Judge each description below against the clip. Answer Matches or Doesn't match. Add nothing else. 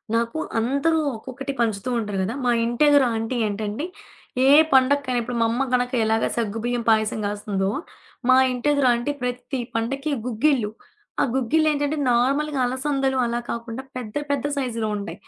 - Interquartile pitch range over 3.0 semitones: Matches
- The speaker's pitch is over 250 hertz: Doesn't match